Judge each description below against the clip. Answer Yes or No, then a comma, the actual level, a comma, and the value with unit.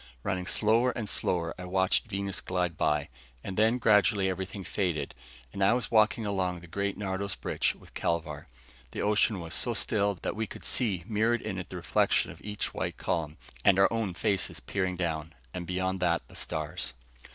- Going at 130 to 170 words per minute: No, average, 185 wpm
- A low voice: Yes, very low, 95 Hz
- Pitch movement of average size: Yes, average, 3.0 semitones